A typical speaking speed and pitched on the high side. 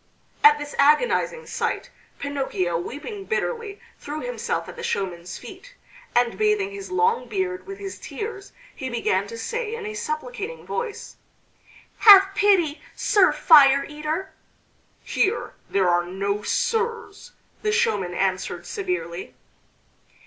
No: slow, 125 wpm; very high, 380 Hz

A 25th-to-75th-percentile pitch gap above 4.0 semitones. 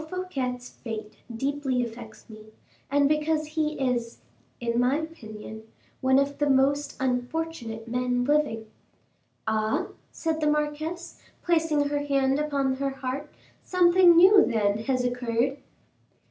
No: average, 3.6 semitones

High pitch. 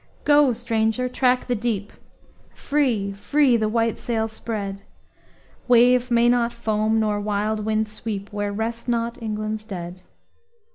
Yes: high, 225 Hz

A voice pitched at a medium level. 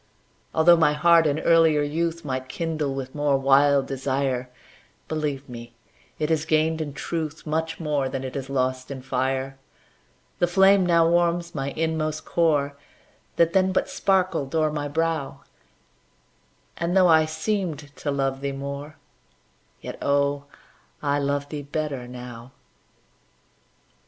Yes: medium, 145 Hz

